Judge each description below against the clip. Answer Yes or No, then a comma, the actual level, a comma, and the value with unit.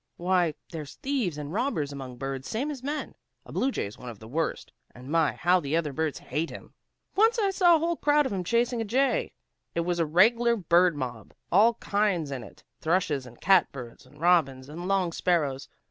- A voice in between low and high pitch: Yes, medium, 175 Hz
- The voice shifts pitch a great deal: Yes, wide, 8.3 semitones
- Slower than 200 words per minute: No, fast, 205 wpm